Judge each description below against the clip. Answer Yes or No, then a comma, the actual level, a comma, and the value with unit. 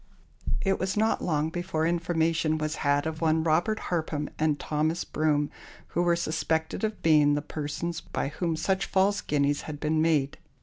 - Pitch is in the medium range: Yes, medium, 160 Hz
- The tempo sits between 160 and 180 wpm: Yes, average, 170 wpm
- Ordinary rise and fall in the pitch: No, narrow, 2.2 semitones